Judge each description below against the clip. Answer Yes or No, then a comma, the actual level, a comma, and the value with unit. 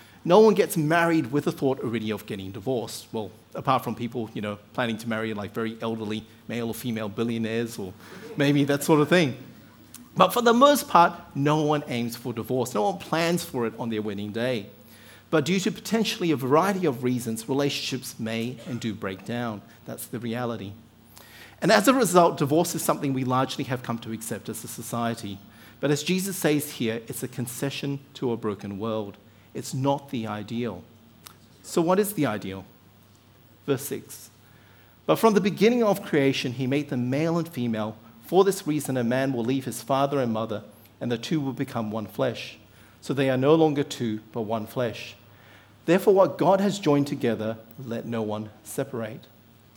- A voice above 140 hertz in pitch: No, low, 120 Hz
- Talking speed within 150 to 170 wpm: No, average, 190 wpm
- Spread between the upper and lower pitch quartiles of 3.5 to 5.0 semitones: Yes, average, 4.7 semitones